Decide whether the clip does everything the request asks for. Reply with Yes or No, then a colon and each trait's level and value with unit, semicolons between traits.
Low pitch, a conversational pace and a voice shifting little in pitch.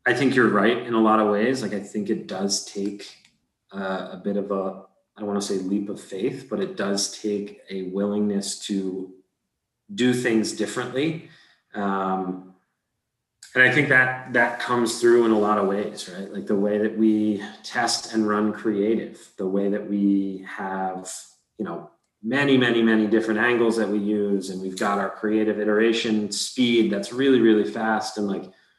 Yes: low, 105 Hz; average, 185 wpm; narrow, 2.3 semitones